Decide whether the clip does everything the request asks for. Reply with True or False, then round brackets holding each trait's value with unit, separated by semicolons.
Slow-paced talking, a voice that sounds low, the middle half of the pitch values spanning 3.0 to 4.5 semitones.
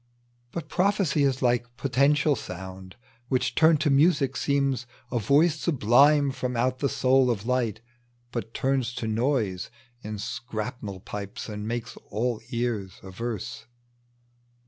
True (130 wpm; 125 Hz; 4.1 semitones)